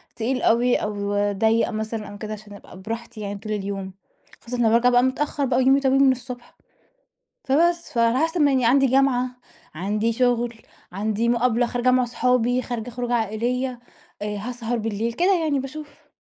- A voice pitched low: No, high, 240 Hz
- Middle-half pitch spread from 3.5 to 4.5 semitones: No, average, 2.8 semitones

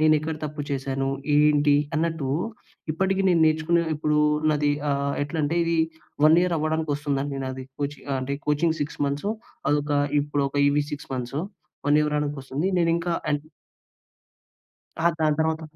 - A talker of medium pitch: Yes, medium, 150 Hz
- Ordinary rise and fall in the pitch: No, narrow, 2.1 semitones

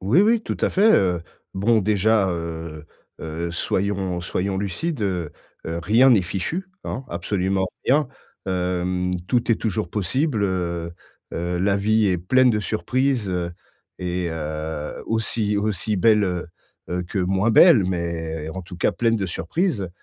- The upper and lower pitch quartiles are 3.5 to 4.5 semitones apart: Yes, average, 4.1 semitones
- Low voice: Yes, very low, 95 Hz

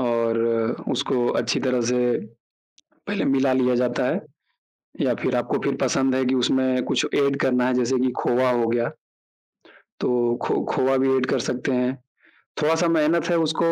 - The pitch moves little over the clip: Yes, narrow, 1.4 semitones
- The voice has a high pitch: No, low, 130 Hz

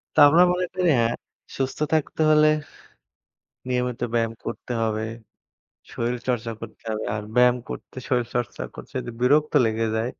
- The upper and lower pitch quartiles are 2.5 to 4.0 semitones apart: Yes, average, 2.8 semitones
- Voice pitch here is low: Yes, low, 125 Hz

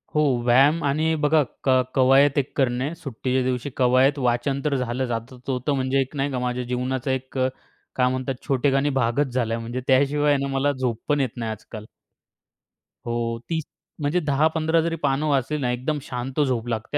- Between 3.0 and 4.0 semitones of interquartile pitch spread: No, narrow, 2.6 semitones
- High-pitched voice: No, low, 130 Hz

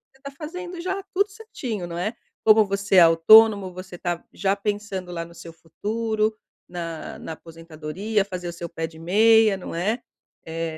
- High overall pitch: Yes, high, 195 Hz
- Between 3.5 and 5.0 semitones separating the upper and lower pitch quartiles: Yes, average, 4.7 semitones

